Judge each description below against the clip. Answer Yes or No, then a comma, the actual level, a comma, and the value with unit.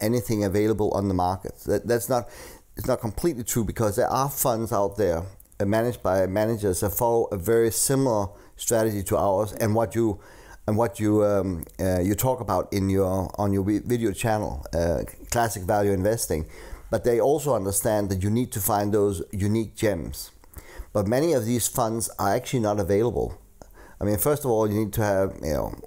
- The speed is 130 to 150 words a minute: No, average, 190 wpm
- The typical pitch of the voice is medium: No, low, 105 Hz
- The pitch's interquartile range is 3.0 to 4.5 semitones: No, narrow, 2.6 semitones